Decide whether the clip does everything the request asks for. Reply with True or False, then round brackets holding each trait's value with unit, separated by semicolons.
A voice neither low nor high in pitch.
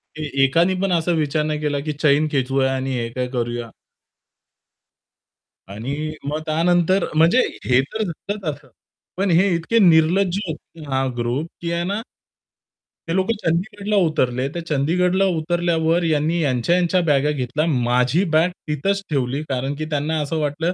True (155 Hz)